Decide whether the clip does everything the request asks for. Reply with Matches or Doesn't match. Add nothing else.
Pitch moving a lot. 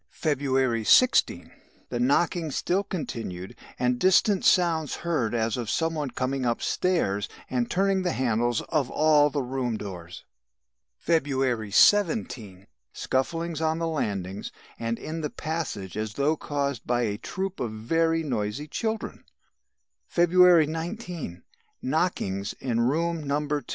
Matches